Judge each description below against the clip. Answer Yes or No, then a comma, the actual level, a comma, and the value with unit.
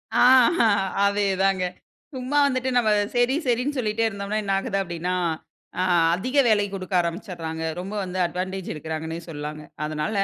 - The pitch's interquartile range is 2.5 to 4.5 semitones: No, average, 4.9 semitones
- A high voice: Yes, high, 195 Hz